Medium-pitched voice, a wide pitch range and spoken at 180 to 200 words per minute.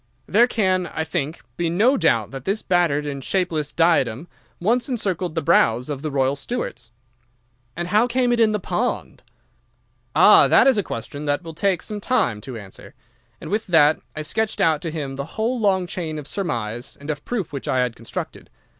Yes: medium, 165 Hz; wide, 6.6 semitones; average, 195 wpm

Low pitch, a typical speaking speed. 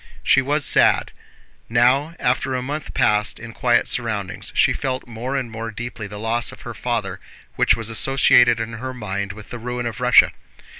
Yes: low, 120 Hz; average, 185 wpm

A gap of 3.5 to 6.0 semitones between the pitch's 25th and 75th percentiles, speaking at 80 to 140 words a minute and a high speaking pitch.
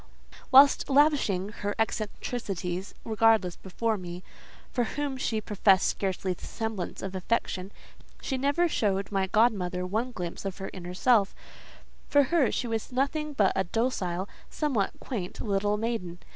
Yes: average, 4.6 semitones; slow, 135 wpm; high, 210 Hz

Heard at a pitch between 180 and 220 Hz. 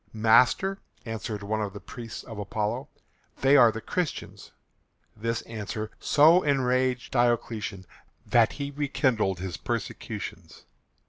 No: low, 115 Hz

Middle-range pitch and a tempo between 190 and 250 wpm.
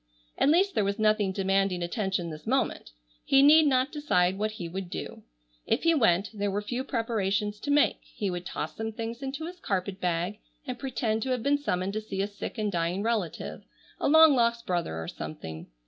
No: high, 210 Hz; fast, 205 wpm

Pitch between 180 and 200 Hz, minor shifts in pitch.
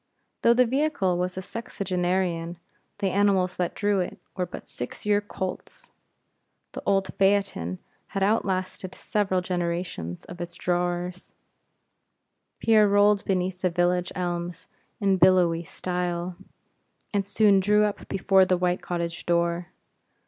Yes: medium, 185 Hz; narrow, 2.2 semitones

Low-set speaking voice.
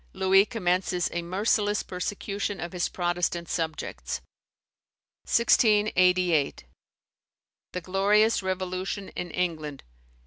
No: medium, 185 Hz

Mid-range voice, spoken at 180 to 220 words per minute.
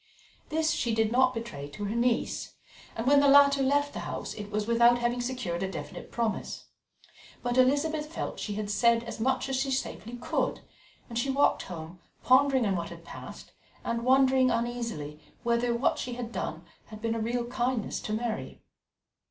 No: high, 240 Hz; average, 185 wpm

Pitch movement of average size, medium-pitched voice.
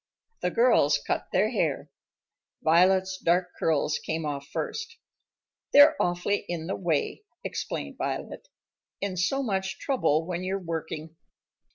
Yes: average, 3.2 semitones; medium, 180 Hz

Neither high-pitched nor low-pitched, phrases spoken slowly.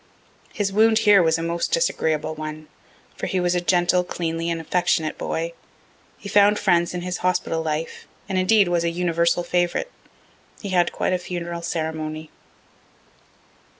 No: medium, 175 Hz; average, 155 wpm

